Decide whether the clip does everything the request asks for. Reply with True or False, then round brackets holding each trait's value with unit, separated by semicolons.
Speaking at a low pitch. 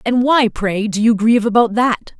False (225 Hz)